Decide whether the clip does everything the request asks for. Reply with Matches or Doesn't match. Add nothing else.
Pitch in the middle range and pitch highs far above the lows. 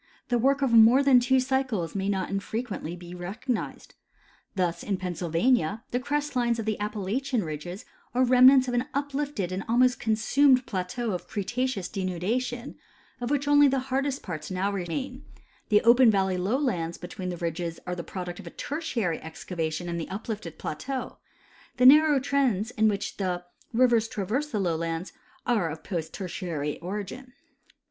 Doesn't match